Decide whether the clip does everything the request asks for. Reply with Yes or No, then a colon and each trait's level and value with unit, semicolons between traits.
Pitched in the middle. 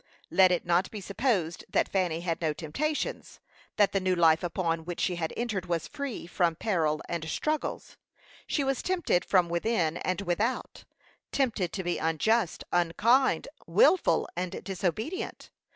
Yes: medium, 180 Hz